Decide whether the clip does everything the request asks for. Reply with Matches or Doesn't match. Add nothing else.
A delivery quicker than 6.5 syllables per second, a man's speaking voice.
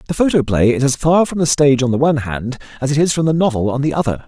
Matches